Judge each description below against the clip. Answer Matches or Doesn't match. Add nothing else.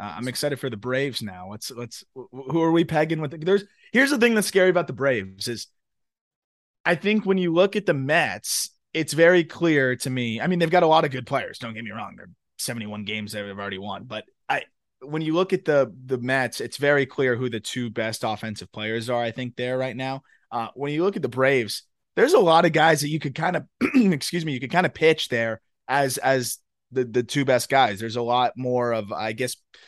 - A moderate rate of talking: Doesn't match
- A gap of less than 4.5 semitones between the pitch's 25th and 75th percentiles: Doesn't match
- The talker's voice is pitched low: Matches